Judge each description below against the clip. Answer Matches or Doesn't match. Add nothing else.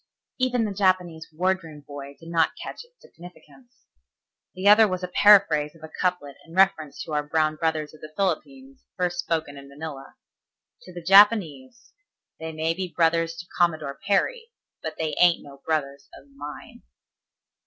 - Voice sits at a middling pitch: Matches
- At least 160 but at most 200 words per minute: Matches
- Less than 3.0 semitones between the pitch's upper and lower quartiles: Doesn't match